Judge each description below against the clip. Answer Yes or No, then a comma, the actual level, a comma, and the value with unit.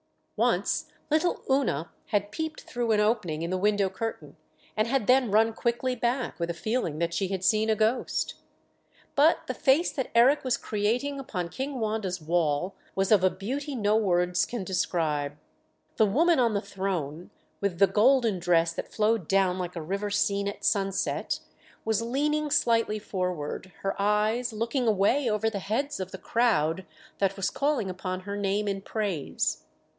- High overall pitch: Yes, high, 205 Hz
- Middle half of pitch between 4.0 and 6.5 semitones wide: Yes, average, 4.3 semitones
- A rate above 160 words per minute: Yes, average, 170 wpm